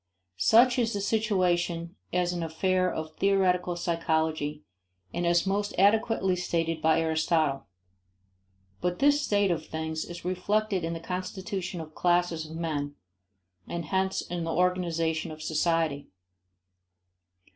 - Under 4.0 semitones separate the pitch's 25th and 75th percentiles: Yes, average, 2.8 semitones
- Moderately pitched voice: Yes, medium, 175 Hz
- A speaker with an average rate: No, slow, 130 wpm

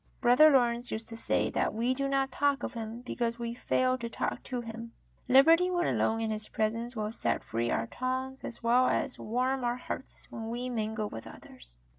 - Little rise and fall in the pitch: Yes, narrow, 2.3 semitones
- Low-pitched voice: No, high, 240 Hz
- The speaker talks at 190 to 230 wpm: Yes, fast, 205 wpm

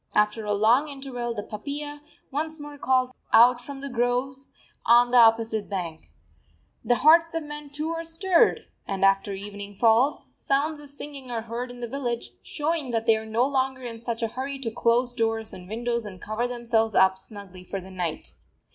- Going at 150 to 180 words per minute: No, average, 190 wpm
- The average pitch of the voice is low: No, high, 240 Hz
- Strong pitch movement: No, average, 4.1 semitones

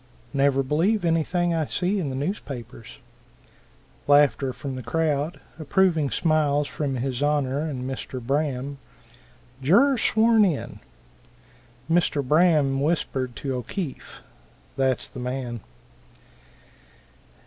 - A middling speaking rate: No, slow, 105 wpm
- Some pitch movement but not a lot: Yes, average, 3.8 semitones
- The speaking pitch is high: No, medium, 145 Hz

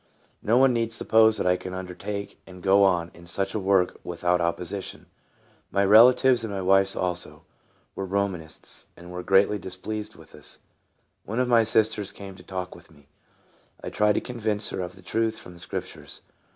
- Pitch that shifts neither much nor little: Yes, average, 3.1 semitones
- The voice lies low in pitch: Yes, very low, 95 Hz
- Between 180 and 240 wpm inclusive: Yes, average, 190 wpm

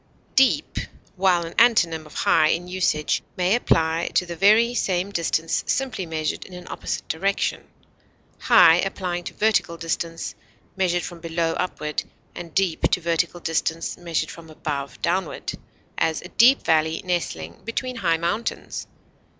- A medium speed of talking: Yes, average, 145 wpm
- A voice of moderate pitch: Yes, medium, 175 Hz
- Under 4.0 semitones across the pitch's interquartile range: Yes, average, 2.7 semitones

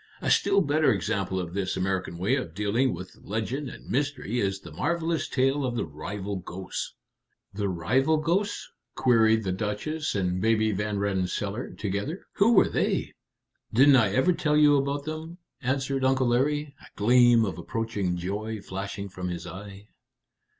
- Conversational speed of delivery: Yes, average, 160 wpm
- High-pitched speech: No, low, 110 Hz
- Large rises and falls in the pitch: Yes, wide, 6.2 semitones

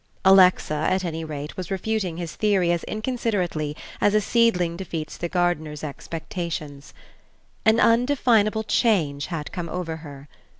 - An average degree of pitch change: Yes, average, 5.0 semitones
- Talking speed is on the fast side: No, slow, 135 wpm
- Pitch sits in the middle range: Yes, medium, 175 Hz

